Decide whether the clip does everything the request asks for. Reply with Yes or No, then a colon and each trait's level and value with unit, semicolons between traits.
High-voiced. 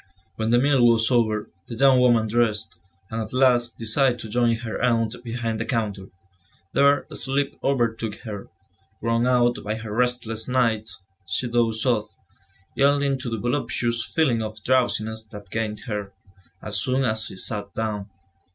No: low, 115 Hz